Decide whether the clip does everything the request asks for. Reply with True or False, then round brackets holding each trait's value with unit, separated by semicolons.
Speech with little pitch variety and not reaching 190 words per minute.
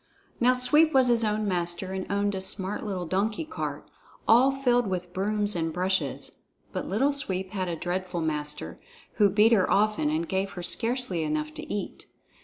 False (4.1 semitones; 180 wpm)